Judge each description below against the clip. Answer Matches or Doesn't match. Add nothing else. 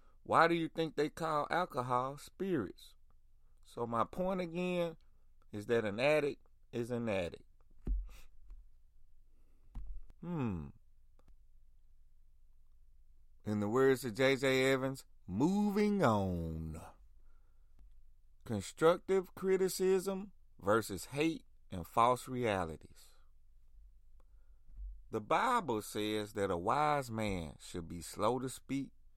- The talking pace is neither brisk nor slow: Doesn't match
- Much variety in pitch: Matches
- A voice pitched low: Matches